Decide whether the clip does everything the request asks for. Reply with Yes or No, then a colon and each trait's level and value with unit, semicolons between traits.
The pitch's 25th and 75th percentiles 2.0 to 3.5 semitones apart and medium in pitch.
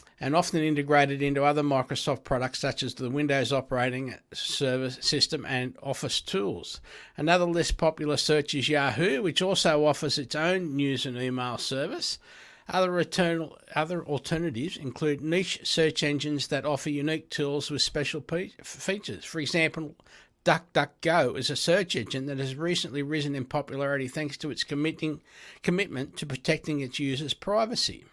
Yes: average, 2.9 semitones; medium, 150 Hz